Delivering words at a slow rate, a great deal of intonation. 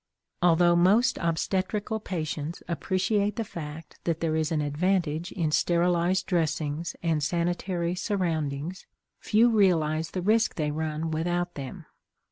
No: slow, 125 wpm; average, 2.9 semitones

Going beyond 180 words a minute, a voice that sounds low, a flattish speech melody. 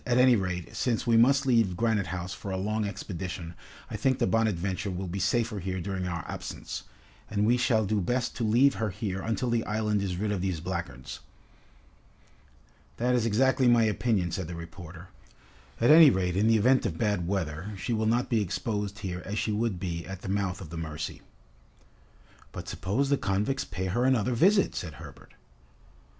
No: average, 190 wpm; low, 100 Hz; average, 4.2 semitones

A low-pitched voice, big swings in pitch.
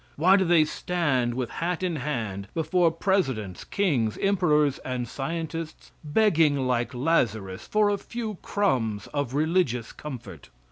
No: medium, 150 Hz; wide, 6.5 semitones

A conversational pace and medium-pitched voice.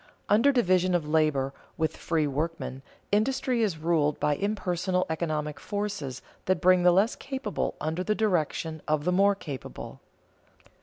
Yes: average, 145 wpm; medium, 175 Hz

